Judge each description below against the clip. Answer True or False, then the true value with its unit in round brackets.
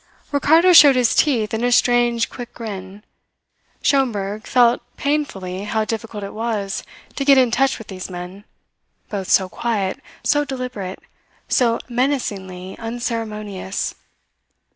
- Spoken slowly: True (125 wpm)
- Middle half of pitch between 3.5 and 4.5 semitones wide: True (4.1 semitones)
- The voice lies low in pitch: False (230 Hz)